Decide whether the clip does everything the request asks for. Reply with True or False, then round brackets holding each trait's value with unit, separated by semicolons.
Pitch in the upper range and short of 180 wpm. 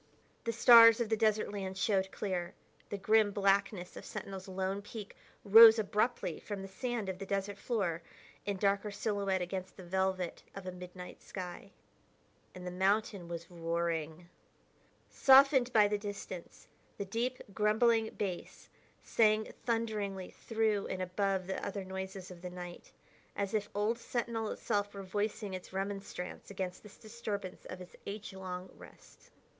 True (200 Hz; 150 wpm)